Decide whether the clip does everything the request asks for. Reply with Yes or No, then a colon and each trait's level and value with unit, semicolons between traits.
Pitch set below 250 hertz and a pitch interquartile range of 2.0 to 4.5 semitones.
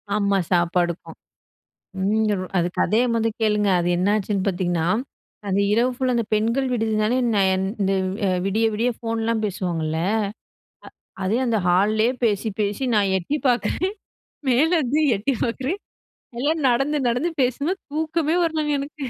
No: high, 220 Hz; average, 5.0 semitones